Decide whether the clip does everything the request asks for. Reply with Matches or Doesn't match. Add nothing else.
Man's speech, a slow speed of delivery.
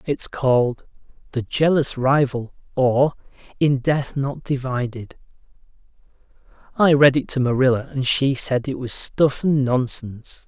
Matches